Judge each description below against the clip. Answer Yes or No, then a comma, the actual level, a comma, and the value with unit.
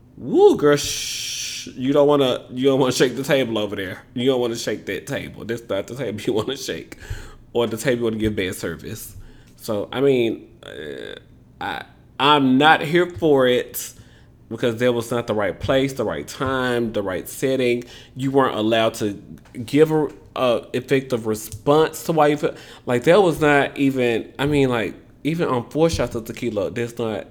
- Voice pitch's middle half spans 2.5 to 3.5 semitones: Yes, average, 3.2 semitones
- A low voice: Yes, low, 125 Hz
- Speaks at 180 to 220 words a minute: Yes, average, 195 wpm